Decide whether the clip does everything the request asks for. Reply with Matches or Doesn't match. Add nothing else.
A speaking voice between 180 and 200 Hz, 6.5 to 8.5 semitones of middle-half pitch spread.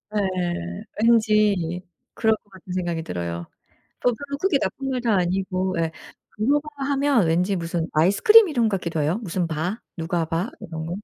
Doesn't match